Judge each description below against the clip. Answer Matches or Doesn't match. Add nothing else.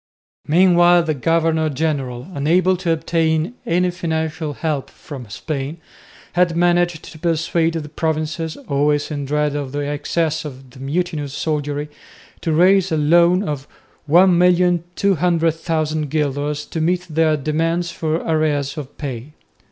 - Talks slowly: Matches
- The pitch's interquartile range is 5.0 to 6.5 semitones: Doesn't match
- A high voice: Doesn't match